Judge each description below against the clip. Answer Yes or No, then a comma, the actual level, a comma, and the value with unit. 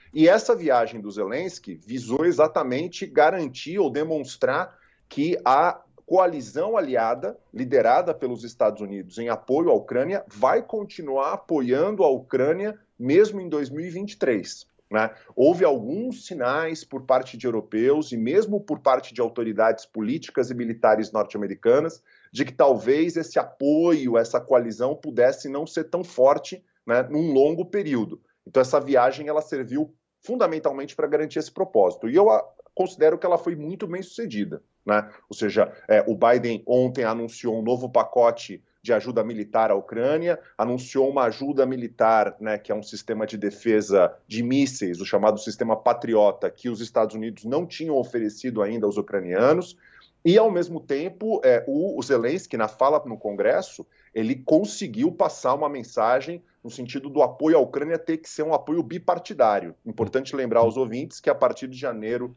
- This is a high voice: No, low, 130 Hz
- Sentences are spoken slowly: No, average, 160 wpm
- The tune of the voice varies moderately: No, wide, 6.0 semitones